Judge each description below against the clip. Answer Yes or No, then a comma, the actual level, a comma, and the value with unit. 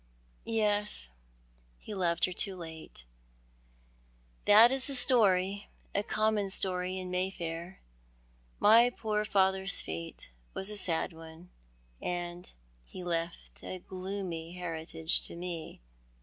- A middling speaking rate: No, slow, 120 wpm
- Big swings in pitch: No, average, 3.3 semitones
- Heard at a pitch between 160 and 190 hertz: Yes, medium, 185 Hz